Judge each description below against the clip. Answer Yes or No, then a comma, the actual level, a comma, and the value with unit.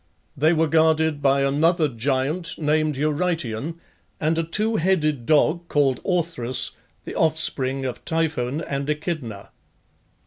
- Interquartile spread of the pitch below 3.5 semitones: Yes, average, 3.1 semitones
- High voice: No, medium, 155 Hz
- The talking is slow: Yes, slow, 125 wpm